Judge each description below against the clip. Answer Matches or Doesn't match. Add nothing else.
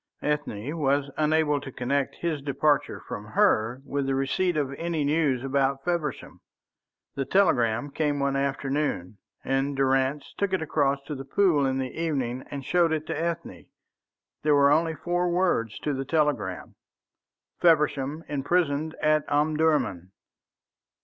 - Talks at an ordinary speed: Matches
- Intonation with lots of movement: Doesn't match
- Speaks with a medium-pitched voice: Matches